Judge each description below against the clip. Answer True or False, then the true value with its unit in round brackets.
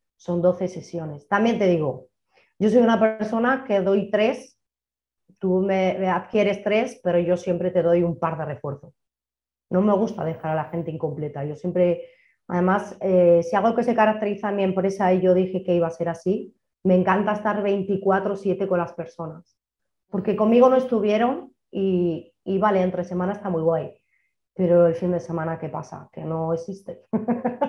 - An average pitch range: True (3.5 semitones)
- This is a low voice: False (185 Hz)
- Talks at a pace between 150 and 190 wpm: True (180 wpm)